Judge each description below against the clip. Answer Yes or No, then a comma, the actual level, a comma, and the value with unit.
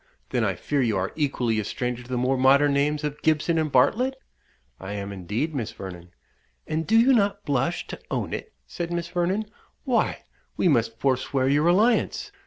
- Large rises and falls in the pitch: Yes, wide, 5.9 semitones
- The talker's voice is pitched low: No, medium, 145 Hz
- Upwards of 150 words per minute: Yes, average, 190 wpm